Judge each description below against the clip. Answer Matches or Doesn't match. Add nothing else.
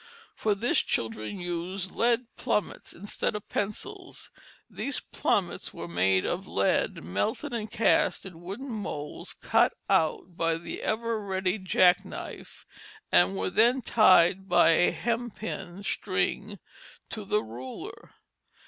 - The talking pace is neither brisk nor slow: Doesn't match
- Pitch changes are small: Doesn't match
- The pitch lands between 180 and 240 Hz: Matches